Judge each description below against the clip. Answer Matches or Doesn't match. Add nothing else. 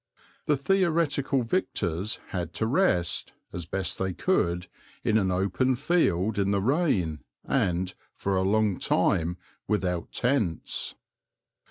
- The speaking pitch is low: Matches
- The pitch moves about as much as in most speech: Doesn't match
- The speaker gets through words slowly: Matches